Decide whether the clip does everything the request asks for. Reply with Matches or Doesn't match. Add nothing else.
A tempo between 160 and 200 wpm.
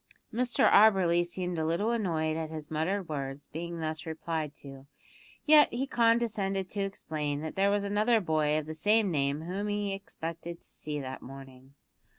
Matches